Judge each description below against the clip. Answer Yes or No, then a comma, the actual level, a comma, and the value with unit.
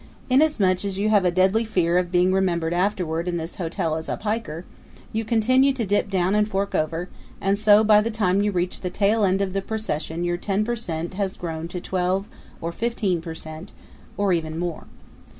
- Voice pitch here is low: No, high, 190 Hz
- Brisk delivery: Yes, fast, 210 wpm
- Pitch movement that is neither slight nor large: Yes, average, 3.4 semitones